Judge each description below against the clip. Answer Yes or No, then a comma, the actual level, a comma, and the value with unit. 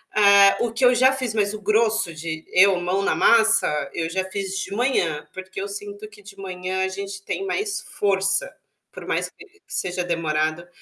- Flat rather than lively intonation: No, average, 3.2 semitones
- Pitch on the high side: Yes, high, 200 Hz